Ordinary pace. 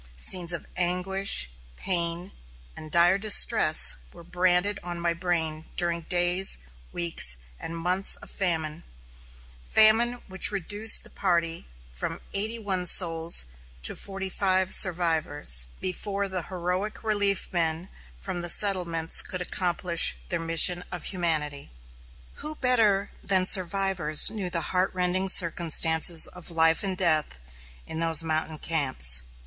No: slow, 130 wpm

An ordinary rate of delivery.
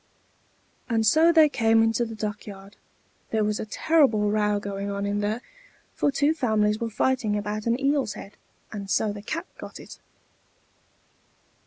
Yes: average, 165 wpm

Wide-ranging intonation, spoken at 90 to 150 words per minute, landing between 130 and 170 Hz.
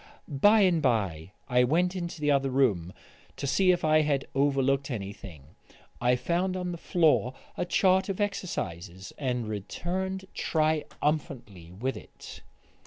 Yes: wide, 7.1 semitones; average, 140 wpm; medium, 140 Hz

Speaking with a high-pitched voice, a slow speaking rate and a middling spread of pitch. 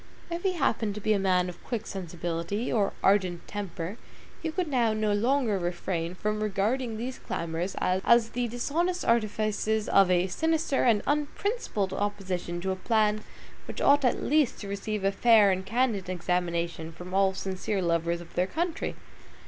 No: high, 205 Hz; average, 165 wpm; average, 4.5 semitones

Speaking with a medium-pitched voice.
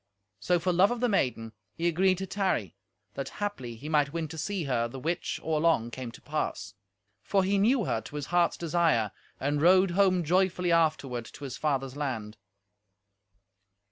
Yes: medium, 160 Hz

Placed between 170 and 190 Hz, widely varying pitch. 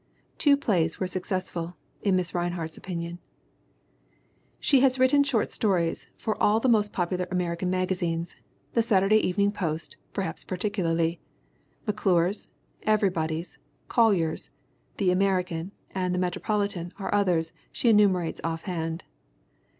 No: medium, 185 Hz; average, 3.4 semitones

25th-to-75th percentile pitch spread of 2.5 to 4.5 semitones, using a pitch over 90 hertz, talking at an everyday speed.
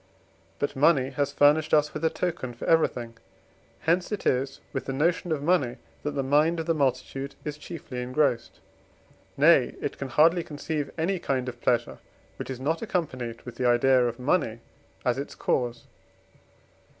Yes: average, 4.1 semitones; medium, 140 Hz; average, 165 wpm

